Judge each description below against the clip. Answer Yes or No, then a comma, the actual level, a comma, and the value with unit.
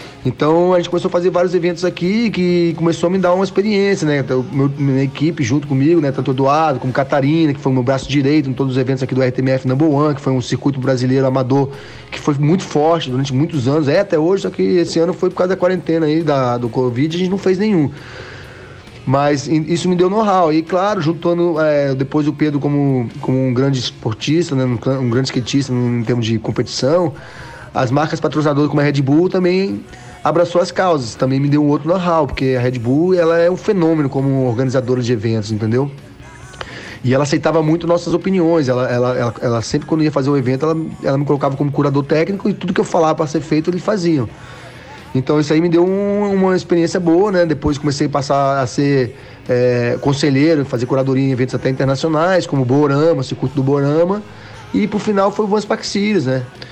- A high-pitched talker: No, medium, 145 Hz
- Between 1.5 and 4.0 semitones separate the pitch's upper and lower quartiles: No, average, 4.4 semitones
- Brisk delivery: Yes, fast, 220 wpm